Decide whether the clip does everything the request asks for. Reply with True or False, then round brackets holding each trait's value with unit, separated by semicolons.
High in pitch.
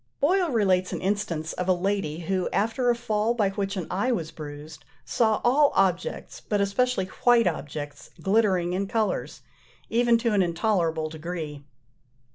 True (195 Hz)